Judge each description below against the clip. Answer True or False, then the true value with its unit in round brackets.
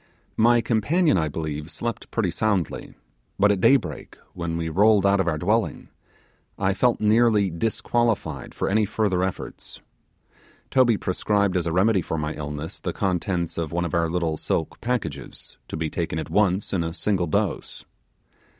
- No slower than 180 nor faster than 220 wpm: False (170 wpm)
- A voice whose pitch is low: True (95 Hz)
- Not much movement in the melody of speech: False (4.6 semitones)